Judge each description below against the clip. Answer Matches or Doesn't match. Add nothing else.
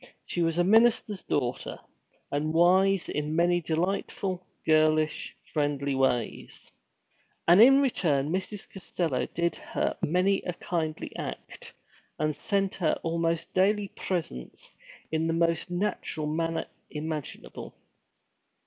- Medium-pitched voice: Matches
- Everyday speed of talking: Doesn't match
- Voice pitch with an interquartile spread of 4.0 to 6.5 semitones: Doesn't match